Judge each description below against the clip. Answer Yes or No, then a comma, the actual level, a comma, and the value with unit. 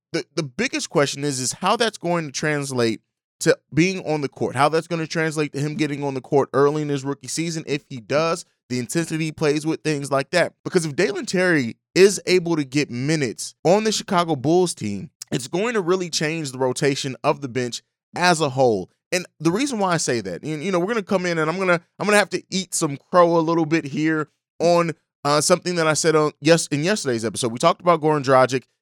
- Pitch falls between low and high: Yes, medium, 160 Hz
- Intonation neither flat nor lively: Yes, average, 3.7 semitones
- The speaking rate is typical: No, fast, 240 wpm